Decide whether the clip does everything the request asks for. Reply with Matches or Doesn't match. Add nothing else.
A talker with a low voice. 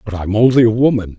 Matches